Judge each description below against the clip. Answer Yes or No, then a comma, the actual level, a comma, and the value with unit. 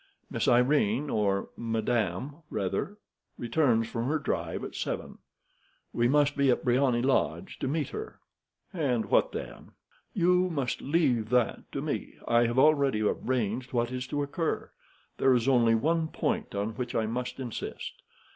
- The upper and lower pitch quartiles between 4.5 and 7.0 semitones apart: No, average, 4.0 semitones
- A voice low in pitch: Yes, low, 125 Hz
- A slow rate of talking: No, average, 155 wpm